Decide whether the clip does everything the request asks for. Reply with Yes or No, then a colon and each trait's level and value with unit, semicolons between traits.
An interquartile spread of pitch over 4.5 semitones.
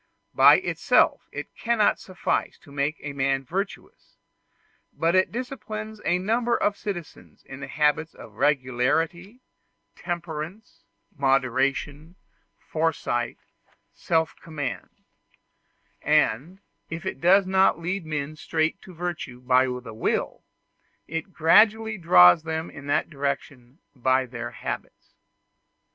Yes: wide, 5.4 semitones